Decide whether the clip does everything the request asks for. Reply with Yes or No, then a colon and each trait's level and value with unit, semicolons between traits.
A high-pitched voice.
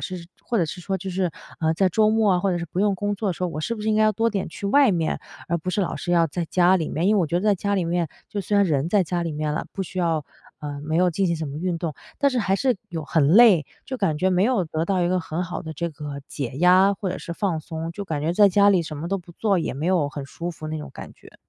No: medium, 180 Hz